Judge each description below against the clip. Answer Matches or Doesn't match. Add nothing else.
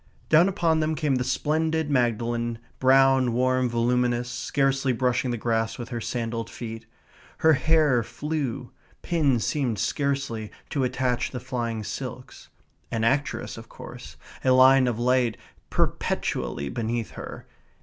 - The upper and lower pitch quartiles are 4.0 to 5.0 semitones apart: Doesn't match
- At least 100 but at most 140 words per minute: Matches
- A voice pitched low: Matches